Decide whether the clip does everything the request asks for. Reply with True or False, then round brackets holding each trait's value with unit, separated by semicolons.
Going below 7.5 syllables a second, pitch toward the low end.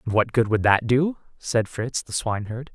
True (4.9 syllables/s; 120 Hz)